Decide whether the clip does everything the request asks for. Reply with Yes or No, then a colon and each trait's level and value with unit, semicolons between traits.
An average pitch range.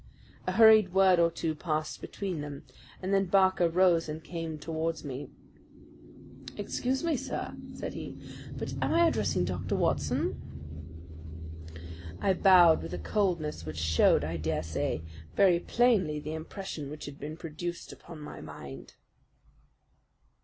Yes: average, 4.4 semitones